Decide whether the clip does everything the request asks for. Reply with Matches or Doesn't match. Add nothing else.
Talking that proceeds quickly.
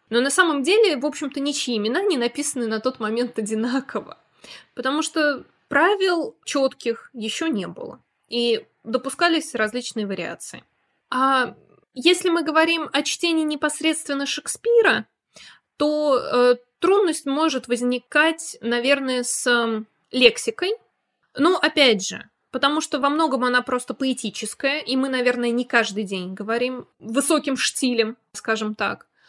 Doesn't match